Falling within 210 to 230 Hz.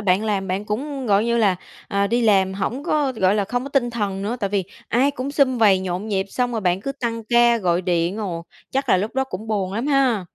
Yes: high, 215 Hz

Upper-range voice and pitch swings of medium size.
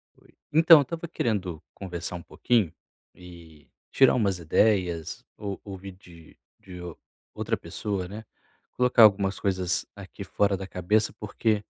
No: very low, 95 Hz; average, 3.2 semitones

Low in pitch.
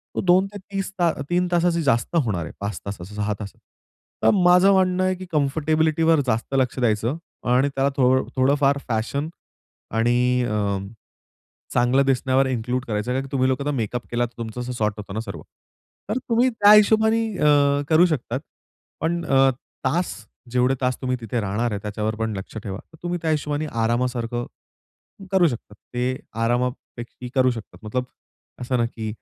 Yes: low, 130 Hz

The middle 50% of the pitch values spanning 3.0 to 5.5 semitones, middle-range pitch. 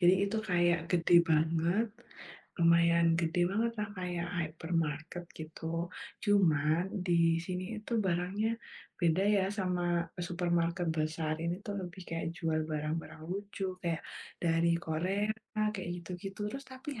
No: narrow, 2.5 semitones; medium, 175 Hz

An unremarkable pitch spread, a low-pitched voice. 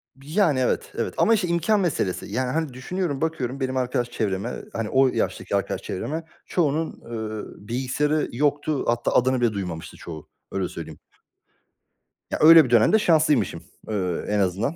No: wide, 5.9 semitones; low, 130 Hz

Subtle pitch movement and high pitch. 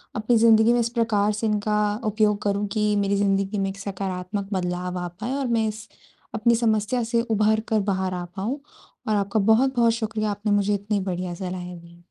Yes: narrow, 2.3 semitones; high, 210 Hz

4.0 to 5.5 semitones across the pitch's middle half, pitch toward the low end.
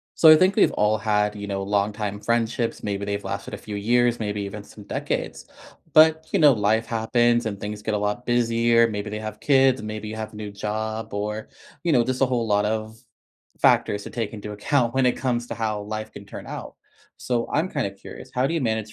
No: narrow, 2.6 semitones; low, 110 Hz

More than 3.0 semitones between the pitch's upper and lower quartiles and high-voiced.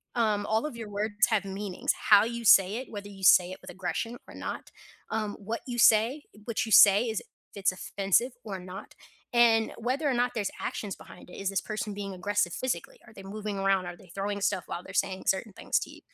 No: narrow, 2.6 semitones; high, 205 Hz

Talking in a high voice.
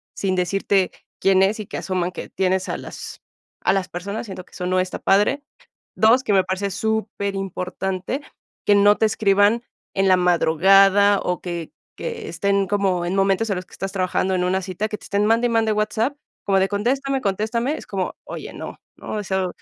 Yes: high, 195 Hz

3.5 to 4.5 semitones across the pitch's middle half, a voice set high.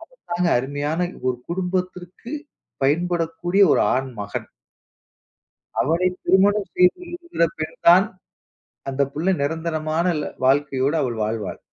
No: average, 4.1 semitones; medium, 165 Hz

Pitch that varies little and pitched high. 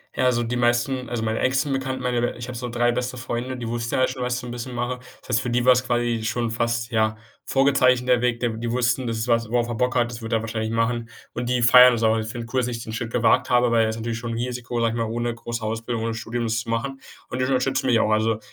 No: narrow, 1.5 semitones; low, 120 Hz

